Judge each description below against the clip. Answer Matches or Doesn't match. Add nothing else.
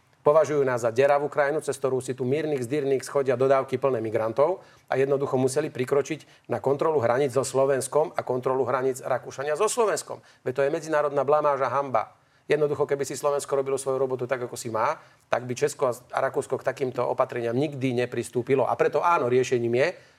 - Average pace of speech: Doesn't match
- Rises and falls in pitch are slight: Matches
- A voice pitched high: Doesn't match